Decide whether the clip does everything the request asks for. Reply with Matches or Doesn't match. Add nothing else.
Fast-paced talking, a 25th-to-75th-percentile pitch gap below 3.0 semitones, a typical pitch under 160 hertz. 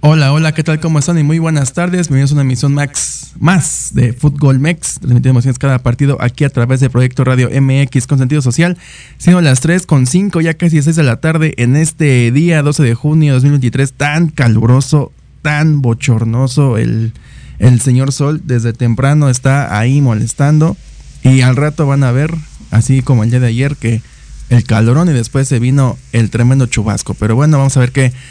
Doesn't match